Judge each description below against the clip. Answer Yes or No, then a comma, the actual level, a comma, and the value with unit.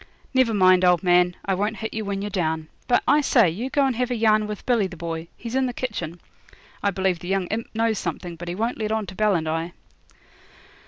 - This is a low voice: No, high, 200 Hz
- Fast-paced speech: Yes, fast, 245 wpm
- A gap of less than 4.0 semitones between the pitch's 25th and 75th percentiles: No, average, 4.3 semitones